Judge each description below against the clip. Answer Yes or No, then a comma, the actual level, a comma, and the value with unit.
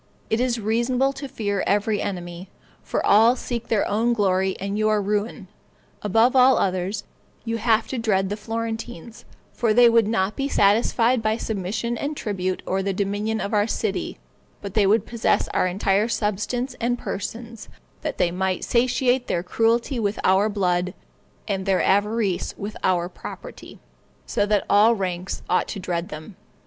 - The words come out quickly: No, average, 165 wpm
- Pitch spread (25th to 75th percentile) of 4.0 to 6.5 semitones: No, average, 3.2 semitones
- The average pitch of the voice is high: Yes, high, 210 Hz